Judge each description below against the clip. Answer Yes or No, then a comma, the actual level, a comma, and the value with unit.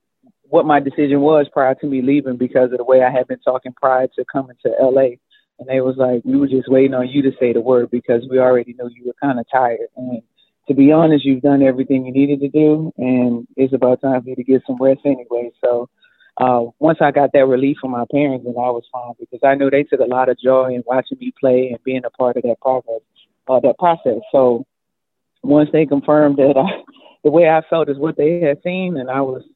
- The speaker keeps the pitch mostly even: Yes, narrow, 2.2 semitones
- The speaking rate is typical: No, fast, 250 wpm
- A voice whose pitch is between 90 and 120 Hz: No, low, 130 Hz